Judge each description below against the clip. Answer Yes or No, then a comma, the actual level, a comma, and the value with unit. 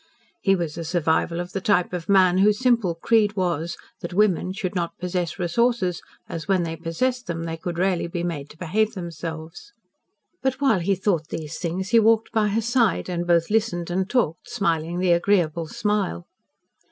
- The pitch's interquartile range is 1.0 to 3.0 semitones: No, average, 3.7 semitones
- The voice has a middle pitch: Yes, medium, 180 Hz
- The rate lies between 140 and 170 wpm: No, average, 185 wpm